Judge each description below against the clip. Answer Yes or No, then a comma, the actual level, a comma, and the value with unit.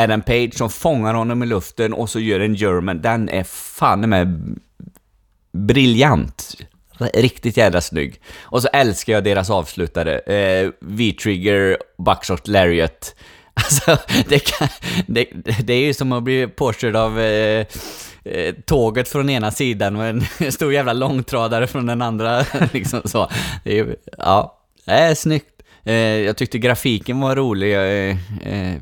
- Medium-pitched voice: No, low, 115 Hz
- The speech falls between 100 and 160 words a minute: Yes, average, 150 wpm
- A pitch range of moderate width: Yes, average, 4.0 semitones